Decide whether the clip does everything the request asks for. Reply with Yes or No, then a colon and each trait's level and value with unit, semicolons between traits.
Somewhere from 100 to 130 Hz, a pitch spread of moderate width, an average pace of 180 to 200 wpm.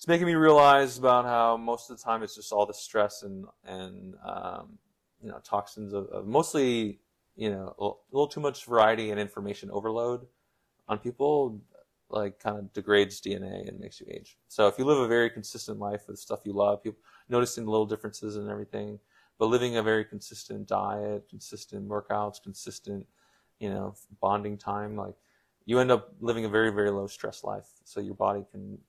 Yes: low, 105 Hz; average, 3.0 semitones; average, 190 wpm